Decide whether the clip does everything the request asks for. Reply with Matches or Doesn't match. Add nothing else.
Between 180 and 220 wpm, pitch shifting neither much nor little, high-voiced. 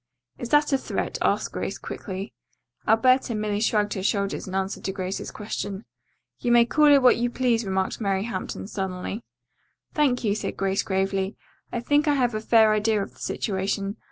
Matches